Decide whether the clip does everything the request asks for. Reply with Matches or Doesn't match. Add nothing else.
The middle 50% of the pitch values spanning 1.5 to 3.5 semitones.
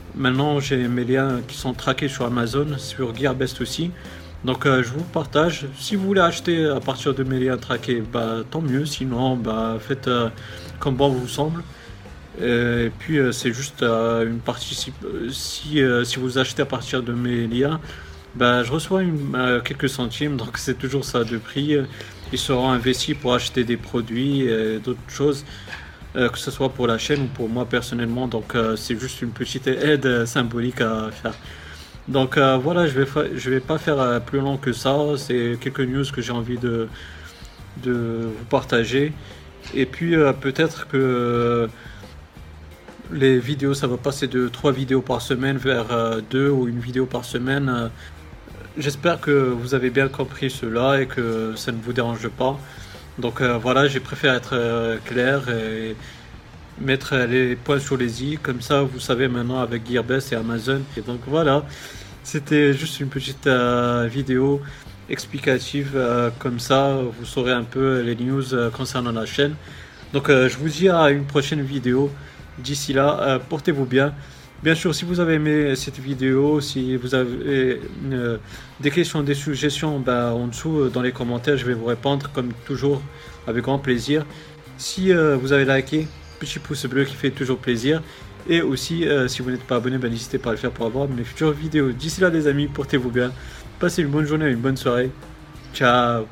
Matches